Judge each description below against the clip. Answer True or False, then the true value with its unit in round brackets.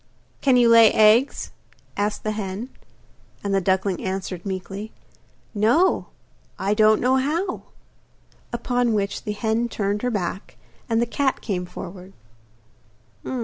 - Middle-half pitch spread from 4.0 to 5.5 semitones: False (3.5 semitones)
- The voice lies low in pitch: False (215 Hz)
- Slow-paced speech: True (130 wpm)